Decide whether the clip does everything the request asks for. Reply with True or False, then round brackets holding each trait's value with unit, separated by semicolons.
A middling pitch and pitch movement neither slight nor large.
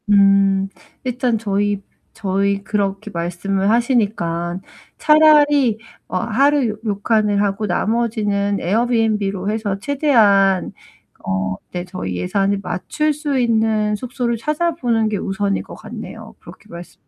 False (210 Hz; 3.3 semitones)